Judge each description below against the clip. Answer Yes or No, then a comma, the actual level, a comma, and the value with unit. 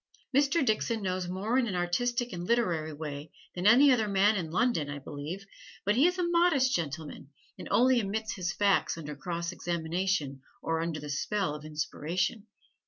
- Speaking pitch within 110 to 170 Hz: No, medium, 185 Hz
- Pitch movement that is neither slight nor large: No, wide, 6.5 semitones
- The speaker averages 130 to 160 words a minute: No, average, 175 wpm